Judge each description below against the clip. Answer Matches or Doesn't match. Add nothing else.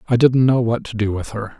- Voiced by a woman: Doesn't match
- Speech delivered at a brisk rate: Matches